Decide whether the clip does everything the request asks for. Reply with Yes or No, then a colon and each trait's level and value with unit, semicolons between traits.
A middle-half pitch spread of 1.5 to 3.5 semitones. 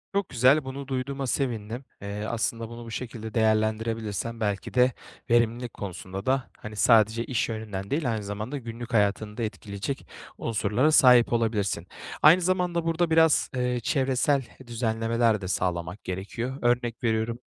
Yes: average, 3.1 semitones